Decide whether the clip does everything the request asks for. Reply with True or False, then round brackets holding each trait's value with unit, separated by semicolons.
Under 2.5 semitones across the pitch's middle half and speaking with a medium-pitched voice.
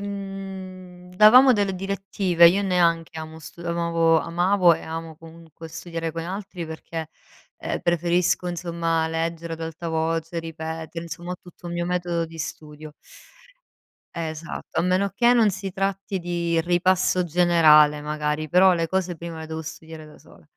True (2.0 semitones; 170 Hz)